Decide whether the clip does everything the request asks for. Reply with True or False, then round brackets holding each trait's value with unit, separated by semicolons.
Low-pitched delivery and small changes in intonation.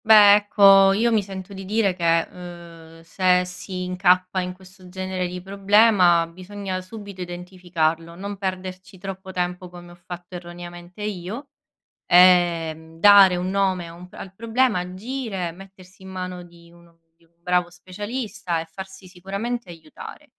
False (185 Hz; 2.0 semitones)